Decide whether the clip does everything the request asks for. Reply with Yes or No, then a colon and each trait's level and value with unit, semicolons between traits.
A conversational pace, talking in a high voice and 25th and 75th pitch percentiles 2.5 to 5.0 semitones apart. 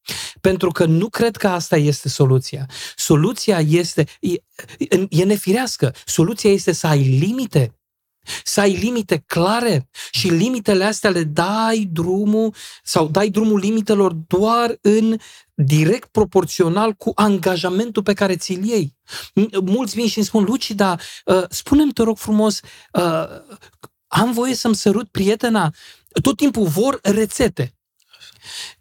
Yes: average, 130 wpm; high, 200 Hz; average, 4.3 semitones